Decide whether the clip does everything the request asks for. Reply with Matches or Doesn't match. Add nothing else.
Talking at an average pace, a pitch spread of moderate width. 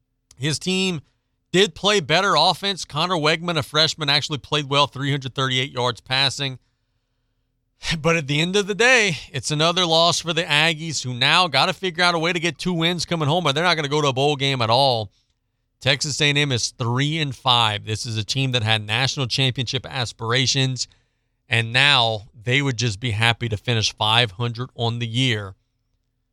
Matches